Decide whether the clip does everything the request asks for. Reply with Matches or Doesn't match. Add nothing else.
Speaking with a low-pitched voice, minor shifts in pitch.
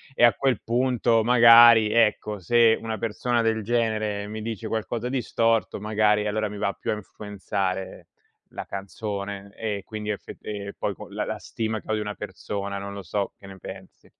Matches